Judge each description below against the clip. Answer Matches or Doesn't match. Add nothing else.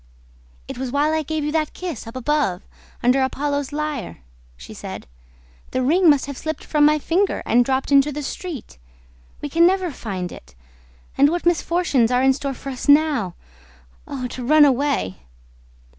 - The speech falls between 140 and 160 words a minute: Doesn't match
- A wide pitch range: Doesn't match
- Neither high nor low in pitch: Doesn't match